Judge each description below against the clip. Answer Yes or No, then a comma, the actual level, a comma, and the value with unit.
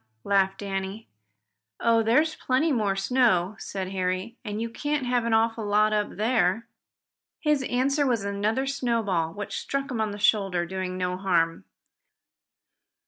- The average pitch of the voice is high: Yes, high, 215 Hz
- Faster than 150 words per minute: No, average, 145 wpm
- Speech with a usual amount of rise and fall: Yes, average, 4.2 semitones